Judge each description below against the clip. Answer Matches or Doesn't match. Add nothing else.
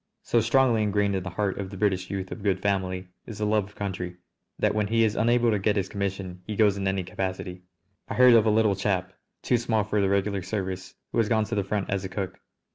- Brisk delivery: Matches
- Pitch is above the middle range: Doesn't match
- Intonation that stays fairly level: Matches